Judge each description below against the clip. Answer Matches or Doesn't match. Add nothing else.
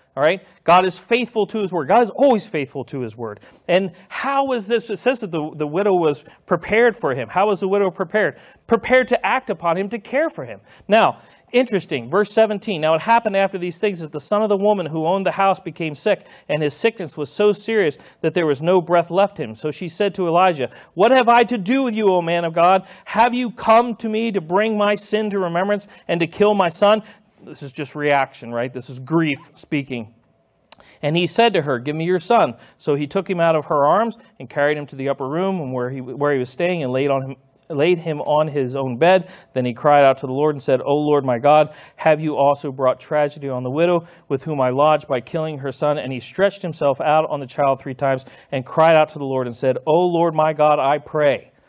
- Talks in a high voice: Doesn't match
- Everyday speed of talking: Doesn't match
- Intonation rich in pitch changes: Matches